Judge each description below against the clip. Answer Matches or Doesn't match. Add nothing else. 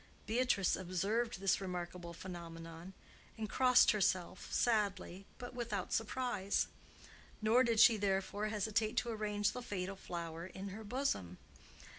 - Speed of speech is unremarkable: Doesn't match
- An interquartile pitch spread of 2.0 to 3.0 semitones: Doesn't match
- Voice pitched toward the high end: Matches